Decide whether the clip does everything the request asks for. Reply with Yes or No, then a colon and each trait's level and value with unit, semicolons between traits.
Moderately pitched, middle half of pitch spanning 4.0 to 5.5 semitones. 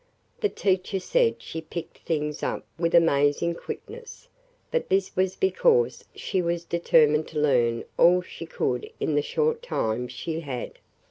Yes: medium, 170 Hz; average, 4.6 semitones